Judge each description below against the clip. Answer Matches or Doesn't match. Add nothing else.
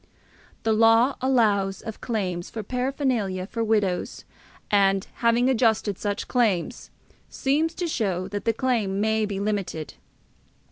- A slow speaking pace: Matches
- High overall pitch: Matches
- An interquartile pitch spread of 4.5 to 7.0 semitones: Doesn't match